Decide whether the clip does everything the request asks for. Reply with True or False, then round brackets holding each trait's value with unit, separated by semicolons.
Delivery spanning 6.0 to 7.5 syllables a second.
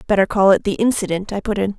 True (6.8 syllables/s)